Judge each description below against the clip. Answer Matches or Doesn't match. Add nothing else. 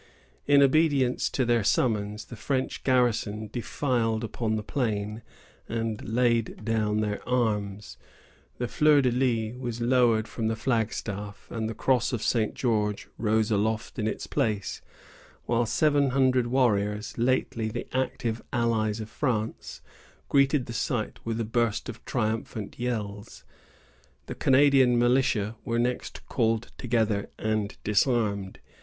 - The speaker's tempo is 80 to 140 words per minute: Matches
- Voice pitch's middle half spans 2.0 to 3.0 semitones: Matches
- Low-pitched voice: Matches